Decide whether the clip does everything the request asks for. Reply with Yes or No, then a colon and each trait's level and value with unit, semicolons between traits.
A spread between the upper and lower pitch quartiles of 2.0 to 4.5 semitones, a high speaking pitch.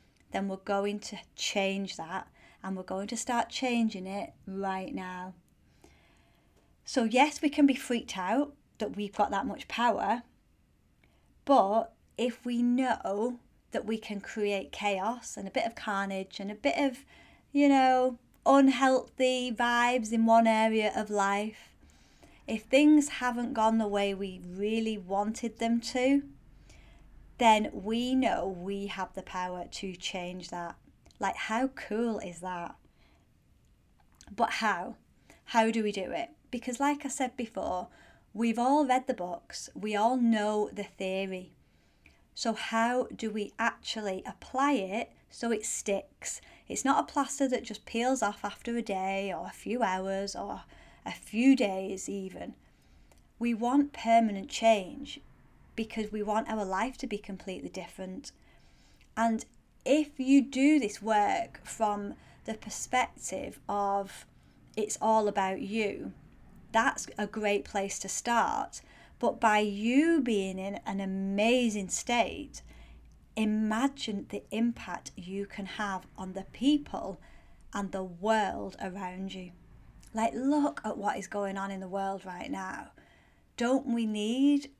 Yes: average, 3.8 semitones; high, 215 Hz